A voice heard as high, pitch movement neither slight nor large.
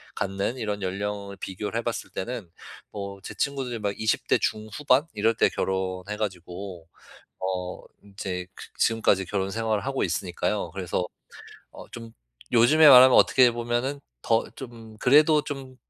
No: low, 105 Hz; average, 4.0 semitones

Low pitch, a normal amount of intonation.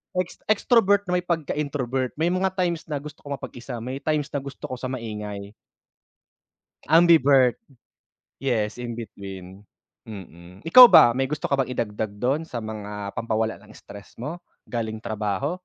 No: low, 125 Hz; wide, 6.0 semitones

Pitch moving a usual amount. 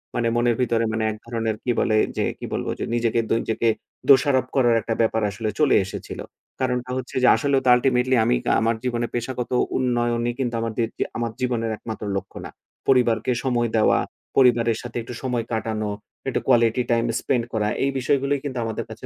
No: narrow, 1.8 semitones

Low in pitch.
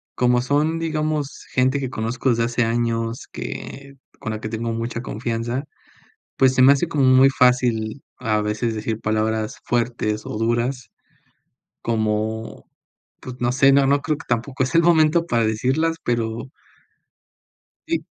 Yes: low, 120 Hz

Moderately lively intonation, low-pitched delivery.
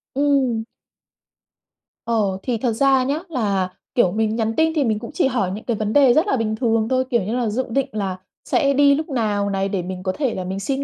No: average, 4.7 semitones; high, 230 Hz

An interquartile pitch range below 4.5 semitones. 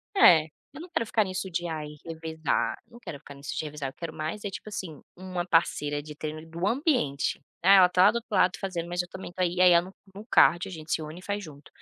Yes: average, 3.4 semitones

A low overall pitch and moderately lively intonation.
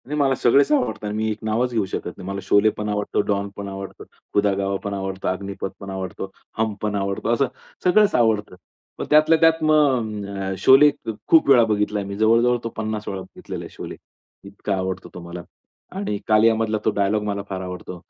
Yes: low, 105 Hz; average, 3.3 semitones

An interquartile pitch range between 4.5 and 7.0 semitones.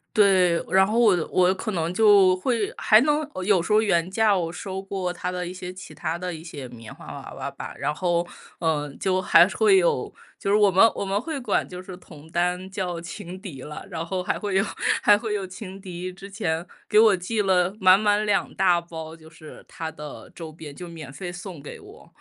No: average, 2.9 semitones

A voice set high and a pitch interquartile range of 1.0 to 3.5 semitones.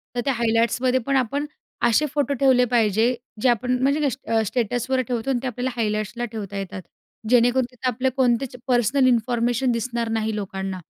Yes: high, 245 Hz; narrow, 2.5 semitones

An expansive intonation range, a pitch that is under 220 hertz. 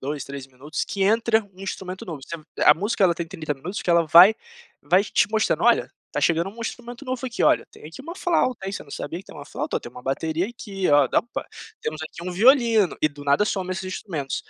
Yes: wide, 6.1 semitones; medium, 185 Hz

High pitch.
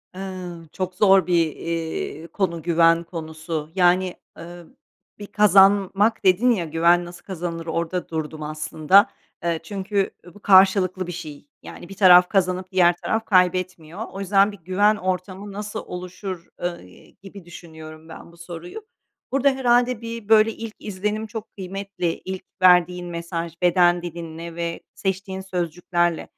No: medium, 180 Hz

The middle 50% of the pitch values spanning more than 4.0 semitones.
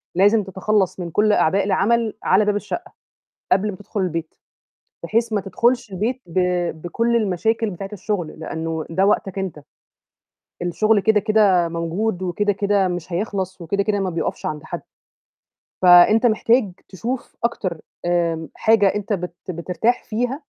No: average, 3.5 semitones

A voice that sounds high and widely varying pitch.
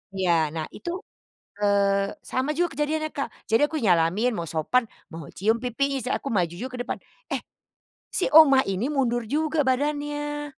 Yes: very high, 250 Hz; wide, 6.8 semitones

